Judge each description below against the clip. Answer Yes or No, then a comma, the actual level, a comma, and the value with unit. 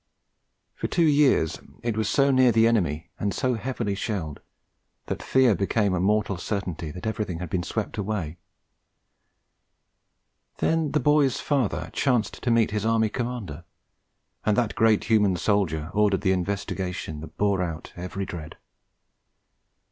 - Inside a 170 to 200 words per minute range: No, average, 150 wpm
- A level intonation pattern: No, average, 4.3 semitones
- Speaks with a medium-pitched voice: No, low, 105 Hz